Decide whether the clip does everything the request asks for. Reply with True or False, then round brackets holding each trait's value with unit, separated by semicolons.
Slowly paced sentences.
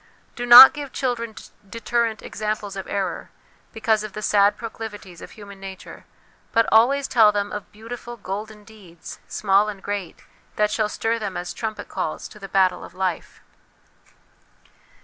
False (160 wpm)